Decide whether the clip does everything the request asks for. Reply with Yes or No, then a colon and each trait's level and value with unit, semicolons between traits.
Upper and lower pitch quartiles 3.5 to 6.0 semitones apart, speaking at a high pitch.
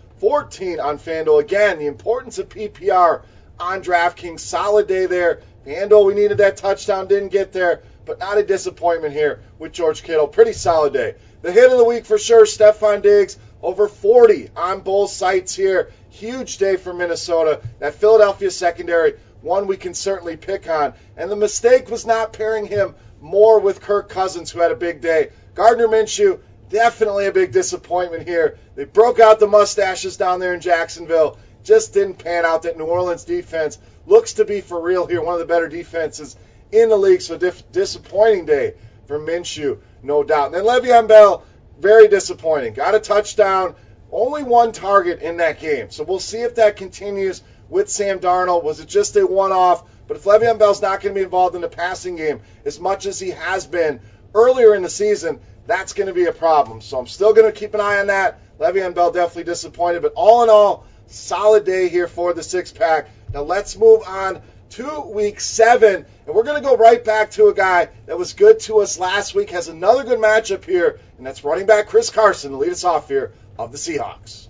Yes: average, 5.2 semitones; high, 200 Hz